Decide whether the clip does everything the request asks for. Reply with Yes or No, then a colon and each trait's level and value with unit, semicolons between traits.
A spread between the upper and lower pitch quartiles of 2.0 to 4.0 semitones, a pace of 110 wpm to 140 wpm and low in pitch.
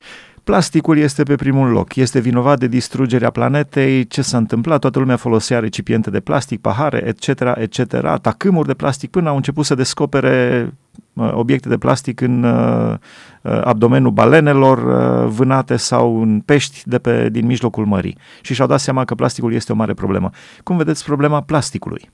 No: average, 3.3 semitones; average, 160 wpm; low, 130 Hz